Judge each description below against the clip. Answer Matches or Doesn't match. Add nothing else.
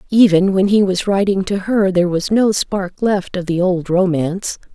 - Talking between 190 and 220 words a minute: Matches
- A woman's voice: Matches